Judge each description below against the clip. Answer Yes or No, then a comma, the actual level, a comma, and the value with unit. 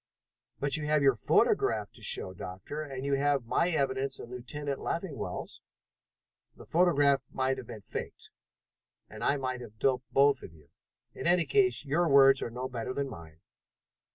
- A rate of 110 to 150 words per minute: No, average, 170 wpm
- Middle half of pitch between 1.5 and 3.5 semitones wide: Yes, narrow, 2.6 semitones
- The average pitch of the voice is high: No, low, 135 Hz